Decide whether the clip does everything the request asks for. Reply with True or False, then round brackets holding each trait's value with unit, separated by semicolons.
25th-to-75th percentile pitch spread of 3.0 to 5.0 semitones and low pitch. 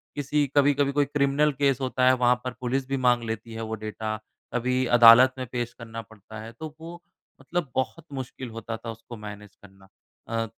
True (3.4 semitones; 125 Hz)